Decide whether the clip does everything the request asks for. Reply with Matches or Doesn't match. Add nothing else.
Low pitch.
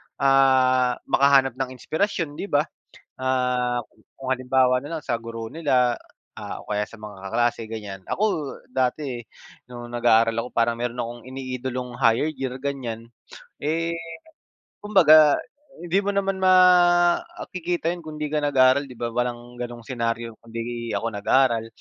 Matches